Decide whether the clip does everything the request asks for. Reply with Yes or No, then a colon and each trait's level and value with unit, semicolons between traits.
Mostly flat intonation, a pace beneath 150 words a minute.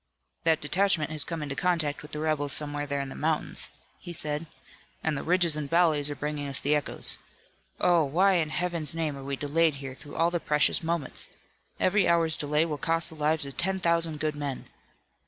No: narrow, 2.3 semitones; fast, 205 wpm